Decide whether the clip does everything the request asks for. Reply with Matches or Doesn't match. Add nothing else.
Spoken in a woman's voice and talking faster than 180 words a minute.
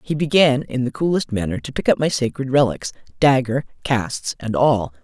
Matches